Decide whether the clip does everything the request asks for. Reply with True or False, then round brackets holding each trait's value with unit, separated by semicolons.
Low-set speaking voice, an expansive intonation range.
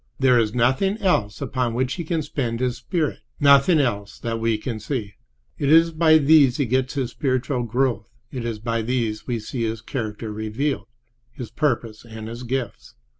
False (125 Hz; 3.6 semitones)